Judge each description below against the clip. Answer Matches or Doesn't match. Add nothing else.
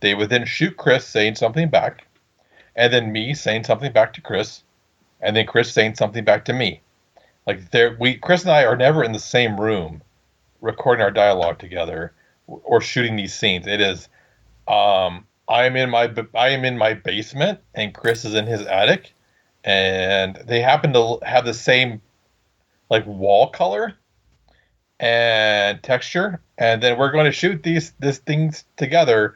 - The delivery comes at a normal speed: Matches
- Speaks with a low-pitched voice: Matches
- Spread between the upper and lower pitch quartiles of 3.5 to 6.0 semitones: Matches